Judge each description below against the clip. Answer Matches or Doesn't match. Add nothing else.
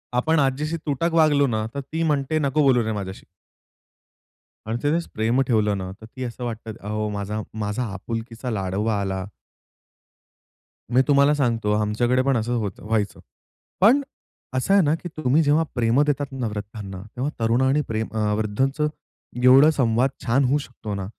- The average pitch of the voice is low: Matches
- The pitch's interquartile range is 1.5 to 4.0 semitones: Doesn't match